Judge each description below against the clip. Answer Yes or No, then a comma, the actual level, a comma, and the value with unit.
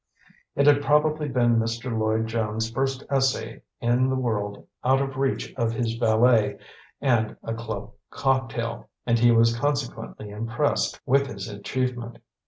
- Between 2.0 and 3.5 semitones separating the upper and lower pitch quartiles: Yes, average, 2.8 semitones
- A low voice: Yes, low, 120 Hz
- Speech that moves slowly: No, average, 145 wpm